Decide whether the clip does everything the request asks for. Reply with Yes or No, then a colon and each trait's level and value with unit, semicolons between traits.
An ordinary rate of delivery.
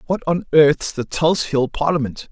Yes: average, 180 wpm